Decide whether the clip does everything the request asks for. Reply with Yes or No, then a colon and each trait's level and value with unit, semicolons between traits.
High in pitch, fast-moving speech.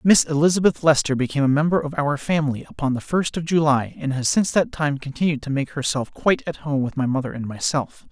No: medium, 145 Hz; fast, 230 wpm